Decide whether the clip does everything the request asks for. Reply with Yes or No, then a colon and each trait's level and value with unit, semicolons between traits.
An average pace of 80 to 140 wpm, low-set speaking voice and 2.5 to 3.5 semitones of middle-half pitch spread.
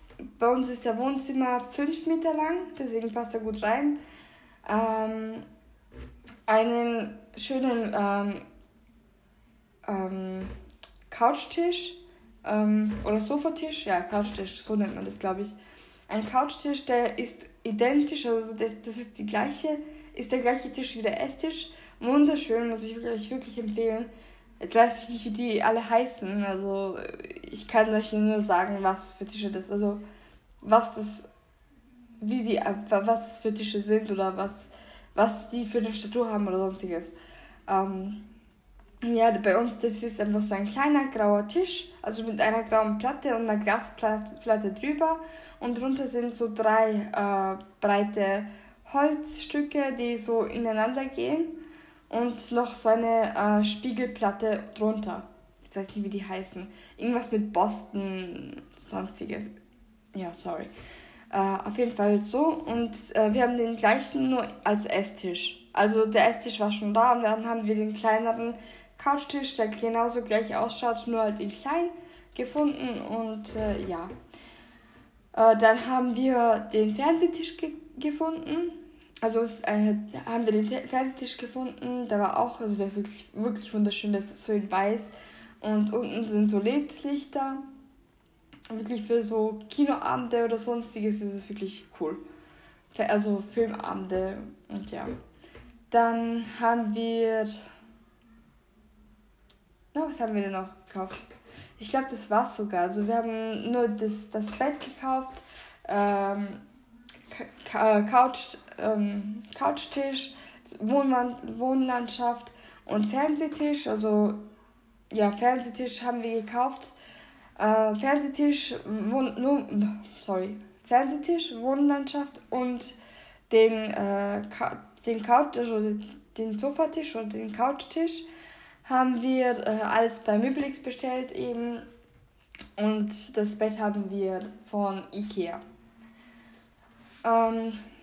No: average, 135 wpm; high, 225 Hz; average, 3.2 semitones